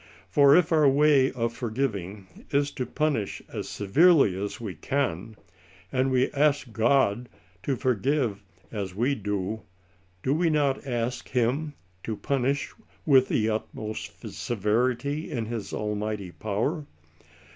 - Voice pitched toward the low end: Yes, low, 125 Hz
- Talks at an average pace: No, slow, 130 wpm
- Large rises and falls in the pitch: No, average, 4.8 semitones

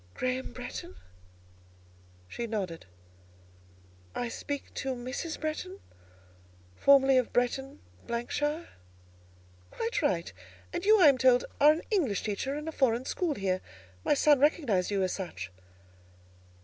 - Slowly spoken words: Yes, slow, 125 wpm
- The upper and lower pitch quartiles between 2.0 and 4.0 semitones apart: No, average, 5.0 semitones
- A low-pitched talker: No, very high, 260 Hz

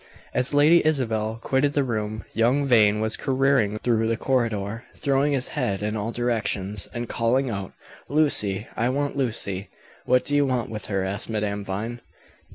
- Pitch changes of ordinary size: Yes, average, 4.1 semitones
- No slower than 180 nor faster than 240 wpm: No, average, 165 wpm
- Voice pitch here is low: Yes, low, 115 Hz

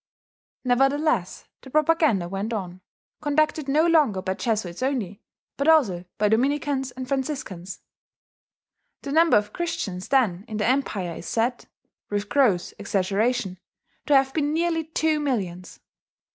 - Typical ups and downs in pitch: No, wide, 6.9 semitones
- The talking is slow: Yes, slow, 130 wpm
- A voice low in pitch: No, very high, 250 Hz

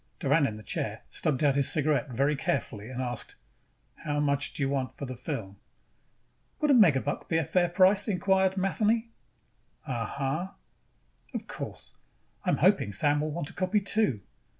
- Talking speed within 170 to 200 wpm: Yes, average, 175 wpm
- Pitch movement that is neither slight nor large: No, wide, 5.9 semitones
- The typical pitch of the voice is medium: Yes, medium, 145 Hz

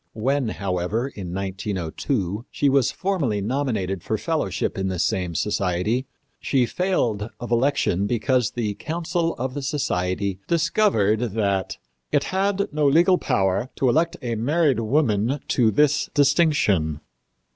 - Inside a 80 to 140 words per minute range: Yes, slow, 135 wpm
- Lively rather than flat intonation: Yes, wide, 6.6 semitones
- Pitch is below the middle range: Yes, low, 120 Hz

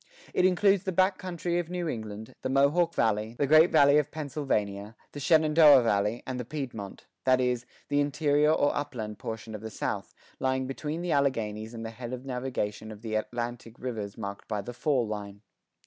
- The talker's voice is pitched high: No, low, 130 Hz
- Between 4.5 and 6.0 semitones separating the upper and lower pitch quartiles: Yes, average, 5.2 semitones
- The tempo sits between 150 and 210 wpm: Yes, average, 190 wpm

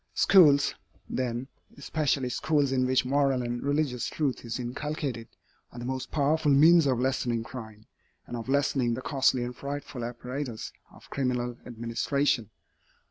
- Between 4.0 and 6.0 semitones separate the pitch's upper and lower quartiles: No, average, 2.8 semitones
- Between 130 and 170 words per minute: Yes, average, 140 wpm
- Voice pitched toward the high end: No, low, 130 Hz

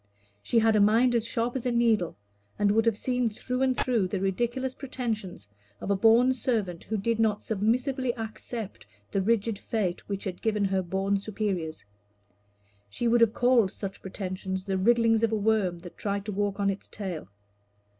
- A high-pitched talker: Yes, high, 215 Hz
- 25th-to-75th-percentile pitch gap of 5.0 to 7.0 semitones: No, average, 3.2 semitones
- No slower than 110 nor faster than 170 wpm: No, average, 185 wpm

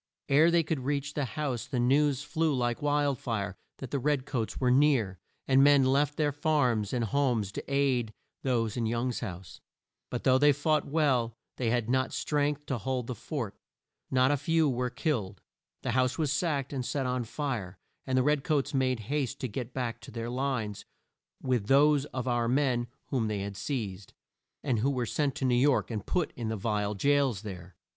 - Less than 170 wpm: No, average, 195 wpm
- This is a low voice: Yes, low, 130 Hz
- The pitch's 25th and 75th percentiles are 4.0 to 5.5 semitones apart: No, average, 3.6 semitones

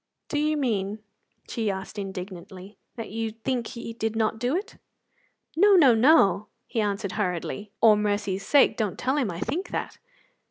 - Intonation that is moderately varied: Yes, average, 4.3 semitones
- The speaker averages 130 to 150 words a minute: No, average, 165 wpm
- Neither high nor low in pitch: No, high, 220 Hz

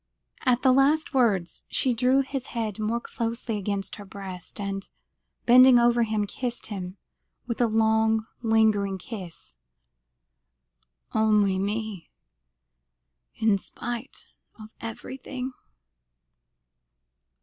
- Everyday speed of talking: No, slow, 105 wpm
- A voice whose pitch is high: Yes, high, 220 Hz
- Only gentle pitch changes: No, average, 3.2 semitones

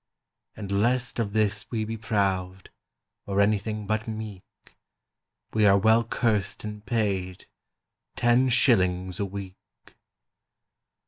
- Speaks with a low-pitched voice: Yes, low, 105 Hz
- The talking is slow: Yes, slow, 115 wpm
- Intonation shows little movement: Yes, narrow, 2.2 semitones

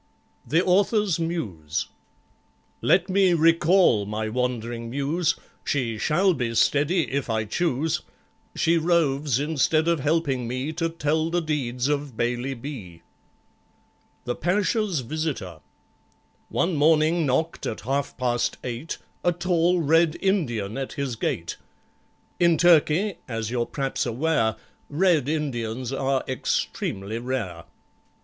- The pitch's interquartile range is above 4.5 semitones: Yes, wide, 5.5 semitones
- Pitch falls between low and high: Yes, medium, 145 Hz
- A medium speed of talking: No, slow, 120 wpm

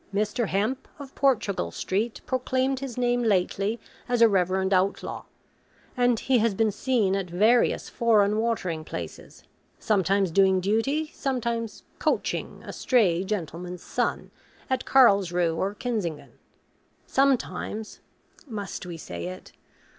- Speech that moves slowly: Yes, slow, 125 wpm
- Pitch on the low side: No, high, 210 Hz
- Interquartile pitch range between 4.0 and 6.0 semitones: Yes, average, 4.5 semitones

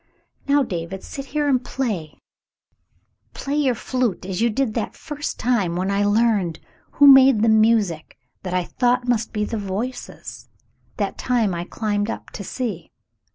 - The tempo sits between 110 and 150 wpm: No, average, 160 wpm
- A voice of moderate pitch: No, high, 225 Hz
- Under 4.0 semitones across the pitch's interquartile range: No, average, 4.8 semitones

